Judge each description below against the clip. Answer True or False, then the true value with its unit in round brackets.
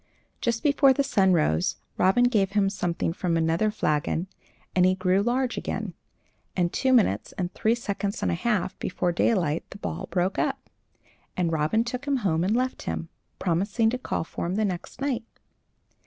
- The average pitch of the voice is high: True (195 Hz)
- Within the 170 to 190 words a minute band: True (180 wpm)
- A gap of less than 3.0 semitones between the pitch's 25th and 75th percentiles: False (5.3 semitones)